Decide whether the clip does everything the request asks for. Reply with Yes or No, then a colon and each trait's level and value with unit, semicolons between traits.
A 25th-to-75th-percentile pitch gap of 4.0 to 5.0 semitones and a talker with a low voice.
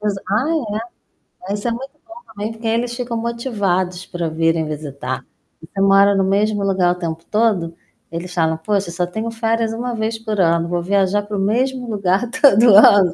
No: average, 4.3 semitones; high, 200 Hz